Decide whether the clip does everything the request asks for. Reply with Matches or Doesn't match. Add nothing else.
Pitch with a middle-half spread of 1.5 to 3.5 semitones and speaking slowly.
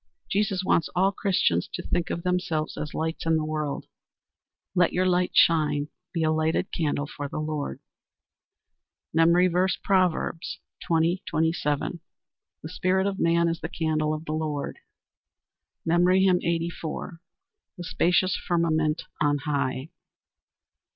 Matches